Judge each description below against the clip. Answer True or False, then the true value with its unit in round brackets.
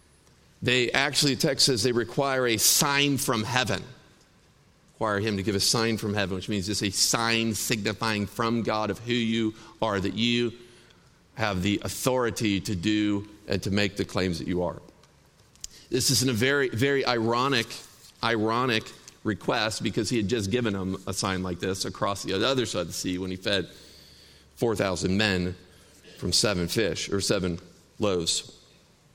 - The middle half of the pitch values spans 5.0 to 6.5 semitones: False (3.8 semitones)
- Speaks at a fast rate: False (175 wpm)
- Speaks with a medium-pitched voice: False (110 Hz)